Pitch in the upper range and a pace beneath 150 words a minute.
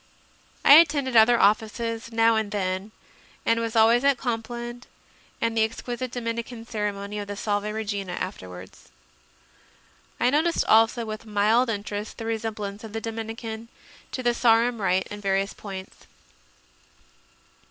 Yes: high, 225 Hz; average, 140 wpm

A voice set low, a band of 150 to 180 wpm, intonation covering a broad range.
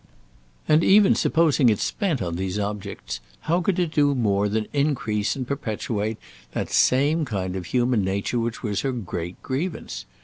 Yes: low, 115 Hz; average, 165 wpm; wide, 6.3 semitones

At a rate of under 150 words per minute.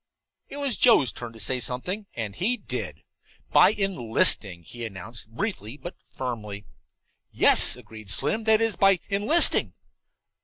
Yes: average, 140 wpm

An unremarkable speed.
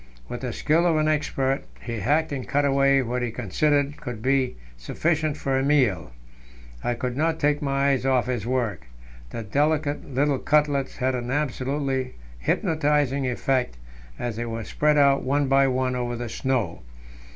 Yes: average, 170 wpm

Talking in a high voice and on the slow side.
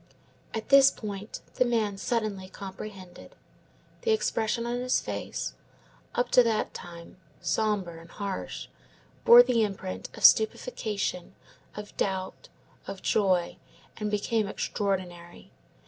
Yes: high, 210 Hz; slow, 115 wpm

